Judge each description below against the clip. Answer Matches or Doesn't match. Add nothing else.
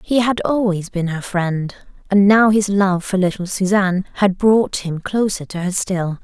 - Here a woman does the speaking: Matches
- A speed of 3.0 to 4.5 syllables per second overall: Matches